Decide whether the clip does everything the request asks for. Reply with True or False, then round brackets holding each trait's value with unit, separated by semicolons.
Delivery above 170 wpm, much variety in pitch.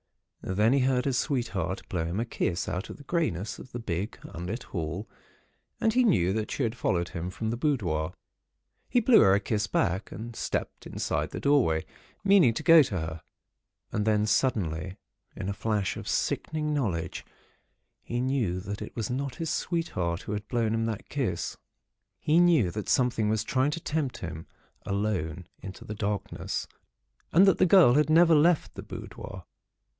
True (180 wpm; 7.0 semitones)